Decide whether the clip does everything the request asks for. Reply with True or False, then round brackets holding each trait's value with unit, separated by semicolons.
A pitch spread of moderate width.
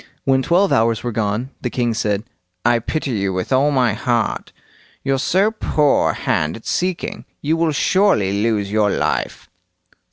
False (5.7 semitones)